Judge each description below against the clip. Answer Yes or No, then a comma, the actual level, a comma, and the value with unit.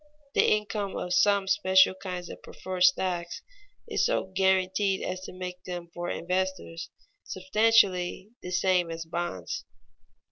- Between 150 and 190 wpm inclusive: No, slow, 135 wpm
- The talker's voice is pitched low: No, medium, 185 Hz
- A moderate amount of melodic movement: No, narrow, 1.2 semitones